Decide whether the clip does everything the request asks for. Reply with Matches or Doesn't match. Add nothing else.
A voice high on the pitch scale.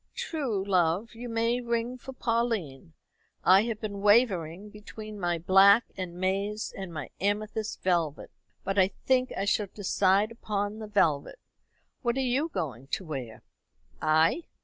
Matches